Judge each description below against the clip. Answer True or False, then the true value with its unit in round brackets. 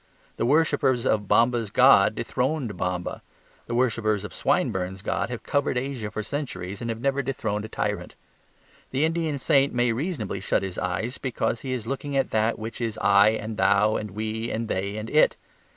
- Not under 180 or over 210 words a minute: True (185 wpm)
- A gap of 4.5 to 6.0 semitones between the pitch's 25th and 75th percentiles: False (4.0 semitones)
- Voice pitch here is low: True (115 Hz)